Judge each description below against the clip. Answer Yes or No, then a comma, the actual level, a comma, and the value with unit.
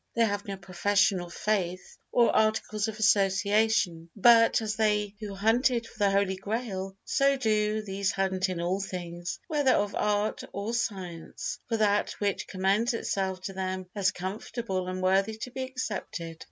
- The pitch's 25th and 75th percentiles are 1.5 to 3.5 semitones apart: Yes, average, 2.7 semitones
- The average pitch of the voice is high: Yes, high, 200 Hz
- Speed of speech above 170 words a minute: No, average, 165 wpm